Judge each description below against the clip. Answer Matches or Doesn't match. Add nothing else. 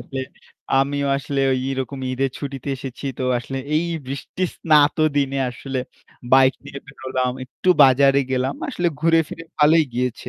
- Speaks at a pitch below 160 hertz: Matches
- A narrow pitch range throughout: Matches